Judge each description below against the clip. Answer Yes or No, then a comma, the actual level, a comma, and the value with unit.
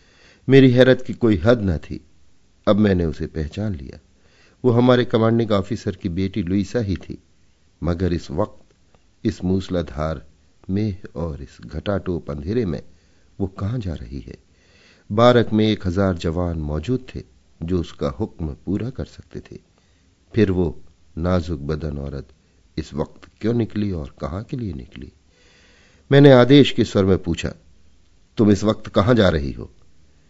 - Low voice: Yes, very low, 90 Hz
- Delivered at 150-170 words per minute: Yes, average, 155 wpm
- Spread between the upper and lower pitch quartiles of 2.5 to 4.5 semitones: No, average, 5.0 semitones